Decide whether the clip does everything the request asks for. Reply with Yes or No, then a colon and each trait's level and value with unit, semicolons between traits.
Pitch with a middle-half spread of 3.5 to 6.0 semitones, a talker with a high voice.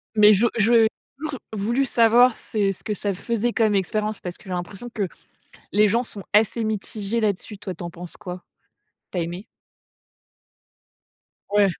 No: average, 2.9 semitones; high, 210 Hz